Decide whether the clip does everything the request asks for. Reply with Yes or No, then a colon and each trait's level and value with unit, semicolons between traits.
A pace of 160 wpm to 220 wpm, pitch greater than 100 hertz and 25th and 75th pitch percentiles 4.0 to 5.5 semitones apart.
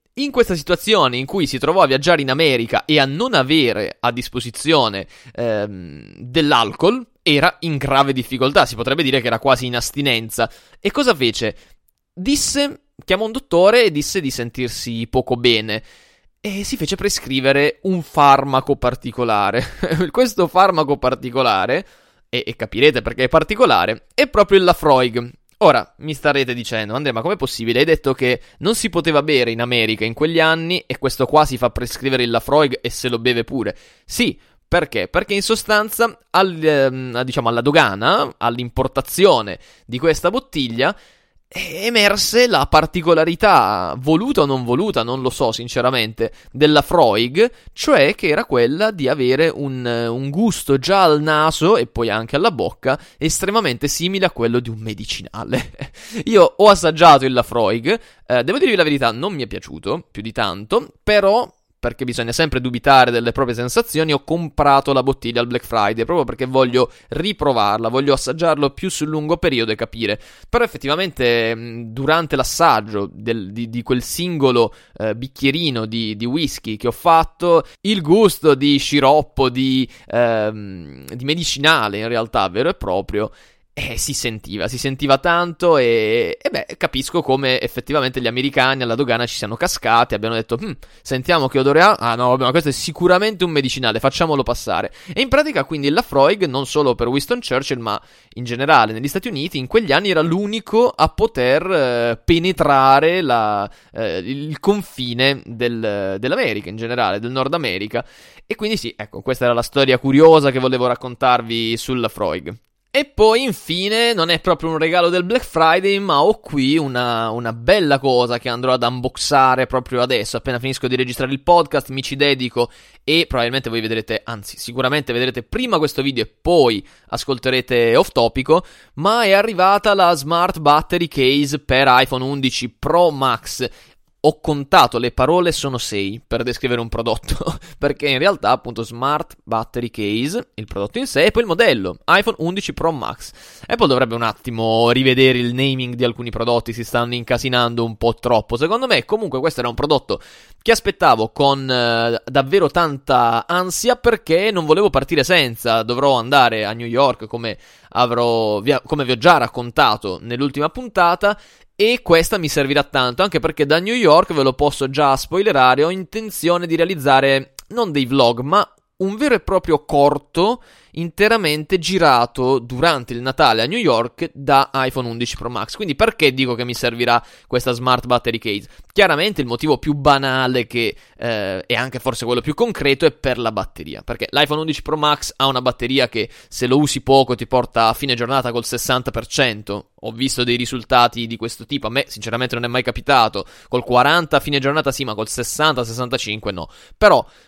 Yes: fast, 170 wpm; low, 135 Hz; average, 5.2 semitones